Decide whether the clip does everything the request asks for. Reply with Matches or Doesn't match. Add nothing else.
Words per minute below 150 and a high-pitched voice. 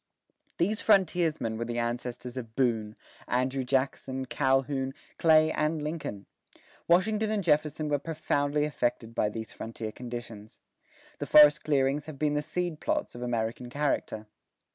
Doesn't match